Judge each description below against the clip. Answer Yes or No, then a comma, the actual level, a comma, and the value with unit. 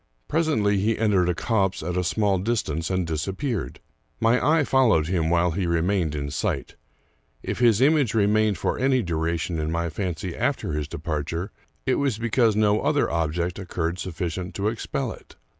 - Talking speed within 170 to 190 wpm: Yes, average, 175 wpm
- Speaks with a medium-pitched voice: No, very low, 95 Hz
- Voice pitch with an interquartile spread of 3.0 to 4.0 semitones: No, average, 5.1 semitones